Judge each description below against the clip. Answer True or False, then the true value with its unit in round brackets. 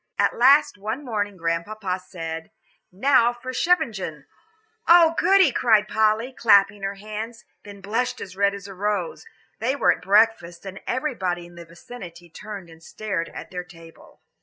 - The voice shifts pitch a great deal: False (4.6 semitones)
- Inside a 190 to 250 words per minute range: False (165 wpm)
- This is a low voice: False (205 Hz)